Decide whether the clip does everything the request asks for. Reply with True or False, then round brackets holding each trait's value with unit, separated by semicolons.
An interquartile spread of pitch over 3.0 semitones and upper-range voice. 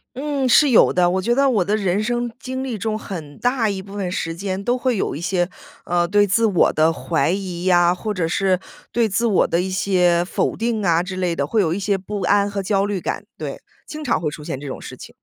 True (4.0 semitones; 195 Hz)